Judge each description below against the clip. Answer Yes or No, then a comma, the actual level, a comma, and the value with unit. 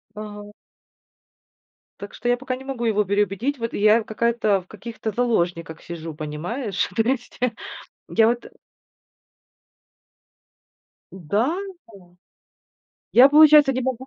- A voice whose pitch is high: Yes, high, 220 Hz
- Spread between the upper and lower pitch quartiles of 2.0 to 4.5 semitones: Yes, average, 3.8 semitones